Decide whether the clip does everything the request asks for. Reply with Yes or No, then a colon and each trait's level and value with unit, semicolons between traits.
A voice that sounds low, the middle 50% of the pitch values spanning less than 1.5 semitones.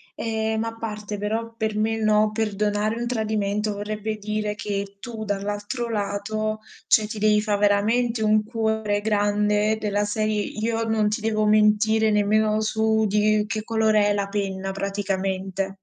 No: high, 215 Hz; narrow, 1.1 semitones